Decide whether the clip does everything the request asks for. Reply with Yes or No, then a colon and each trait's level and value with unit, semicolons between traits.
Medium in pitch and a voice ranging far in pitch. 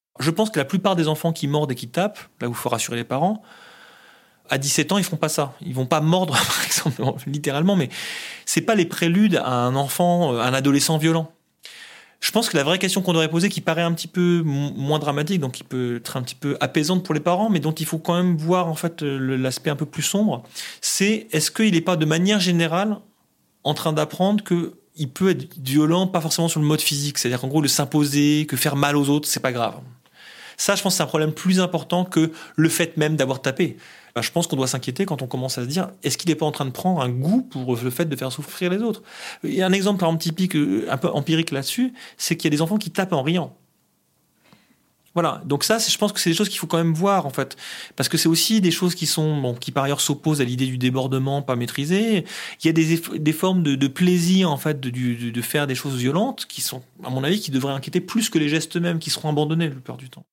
No: medium, 160 Hz; average, 4.3 semitones